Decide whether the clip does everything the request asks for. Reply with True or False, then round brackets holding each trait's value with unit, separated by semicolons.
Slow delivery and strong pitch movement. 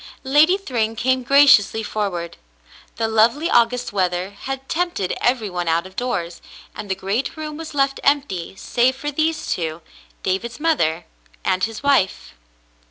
False (150 wpm; 6.7 semitones)